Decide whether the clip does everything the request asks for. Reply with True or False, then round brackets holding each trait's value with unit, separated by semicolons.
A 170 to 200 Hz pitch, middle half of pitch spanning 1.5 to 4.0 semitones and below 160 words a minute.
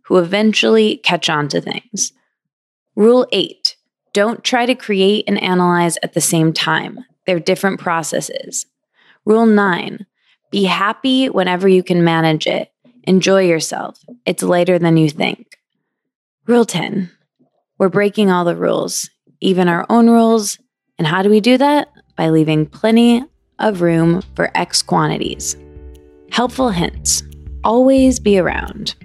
False (190 Hz; 4.7 semitones; 140 wpm)